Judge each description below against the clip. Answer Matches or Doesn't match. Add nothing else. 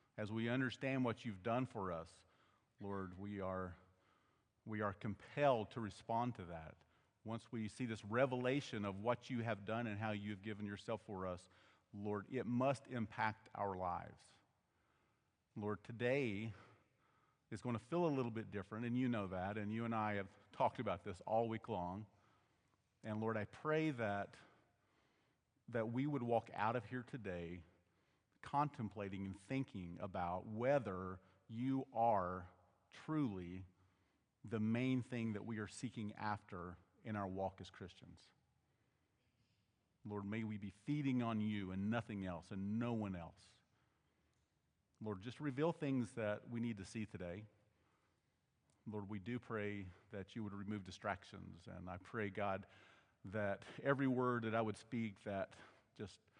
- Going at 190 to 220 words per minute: Doesn't match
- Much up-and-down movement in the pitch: Doesn't match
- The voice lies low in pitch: Matches